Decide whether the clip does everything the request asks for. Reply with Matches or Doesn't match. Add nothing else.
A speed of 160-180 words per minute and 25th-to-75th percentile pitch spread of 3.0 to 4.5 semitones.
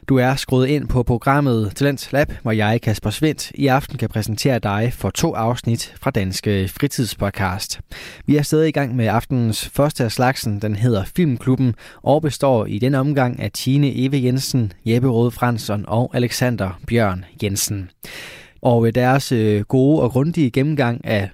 Matches